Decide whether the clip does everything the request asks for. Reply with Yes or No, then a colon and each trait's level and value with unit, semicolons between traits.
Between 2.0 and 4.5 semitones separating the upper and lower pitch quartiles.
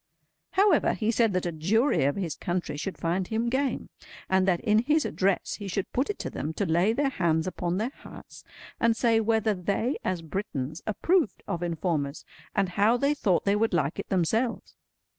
No: average, 4.9 semitones